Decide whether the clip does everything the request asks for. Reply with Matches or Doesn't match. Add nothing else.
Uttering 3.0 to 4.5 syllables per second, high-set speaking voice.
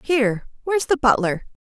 Doesn't match